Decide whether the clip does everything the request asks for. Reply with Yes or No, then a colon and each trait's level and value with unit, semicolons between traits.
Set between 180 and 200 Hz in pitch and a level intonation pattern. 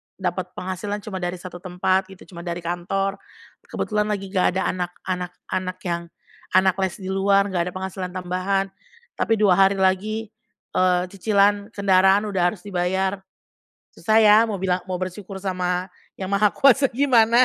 Yes: high, 190 Hz; narrow, 1.9 semitones